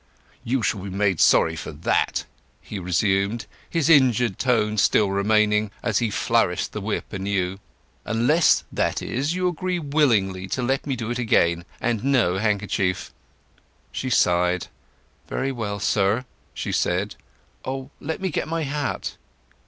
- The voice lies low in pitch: Yes, low, 110 Hz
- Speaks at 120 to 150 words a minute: Yes, average, 145 wpm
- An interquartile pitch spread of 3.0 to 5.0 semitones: No, wide, 5.4 semitones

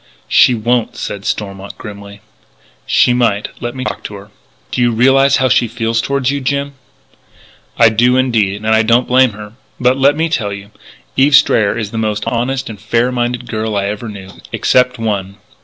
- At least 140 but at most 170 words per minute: No, average, 190 wpm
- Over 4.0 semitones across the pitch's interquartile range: No, average, 3.4 semitones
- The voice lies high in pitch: No, low, 115 Hz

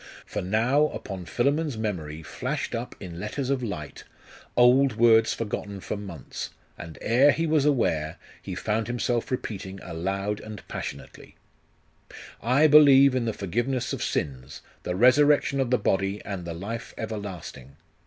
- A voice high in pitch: No, low, 110 Hz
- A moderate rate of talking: Yes, average, 145 wpm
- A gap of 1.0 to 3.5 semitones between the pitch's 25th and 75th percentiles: No, average, 5.2 semitones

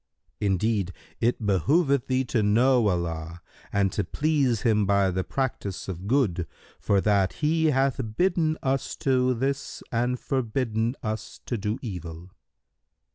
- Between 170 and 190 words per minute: No, slow, 135 wpm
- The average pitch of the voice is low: Yes, low, 115 Hz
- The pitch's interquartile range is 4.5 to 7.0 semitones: Yes, average, 5.2 semitones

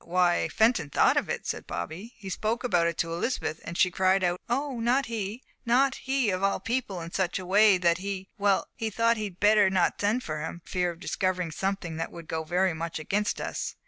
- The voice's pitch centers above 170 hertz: Yes, high, 190 Hz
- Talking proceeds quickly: Yes, fast, 225 wpm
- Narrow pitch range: No, average, 4.4 semitones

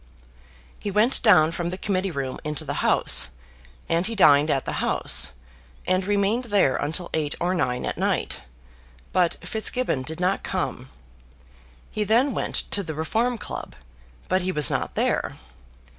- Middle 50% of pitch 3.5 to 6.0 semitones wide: Yes, average, 5.1 semitones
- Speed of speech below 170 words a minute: Yes, average, 160 wpm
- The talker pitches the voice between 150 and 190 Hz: Yes, medium, 185 Hz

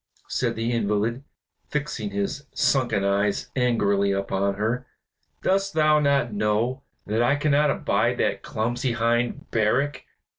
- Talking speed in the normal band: No, slow, 125 wpm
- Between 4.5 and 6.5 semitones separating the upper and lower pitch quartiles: Yes, average, 4.9 semitones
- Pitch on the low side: Yes, low, 115 Hz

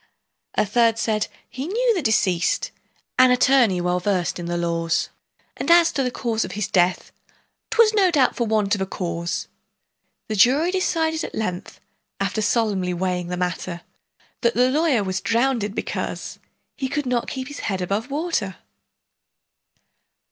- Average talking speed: Yes, average, 160 wpm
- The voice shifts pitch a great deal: Yes, wide, 6.5 semitones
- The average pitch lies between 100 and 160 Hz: No, high, 220 Hz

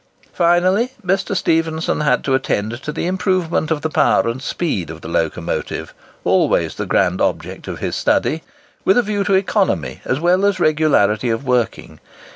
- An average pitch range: No, wide, 7.2 semitones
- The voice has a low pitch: No, medium, 160 Hz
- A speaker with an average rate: Yes, average, 160 wpm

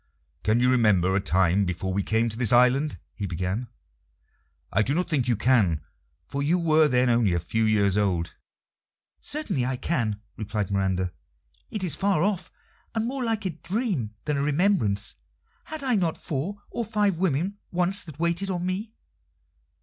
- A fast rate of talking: No, average, 170 wpm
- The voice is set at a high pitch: No, low, 135 Hz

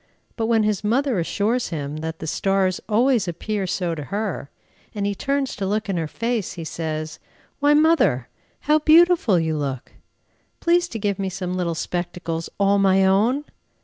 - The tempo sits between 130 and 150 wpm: No, average, 175 wpm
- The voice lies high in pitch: Yes, high, 195 Hz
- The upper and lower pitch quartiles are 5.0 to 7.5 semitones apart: Yes, wide, 5.6 semitones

